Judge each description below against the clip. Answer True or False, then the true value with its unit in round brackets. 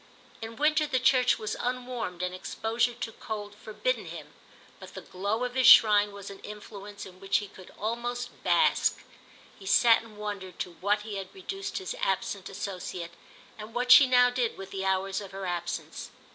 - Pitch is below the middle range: False (210 Hz)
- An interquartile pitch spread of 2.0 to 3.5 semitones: False (4.0 semitones)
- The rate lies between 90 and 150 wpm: False (185 wpm)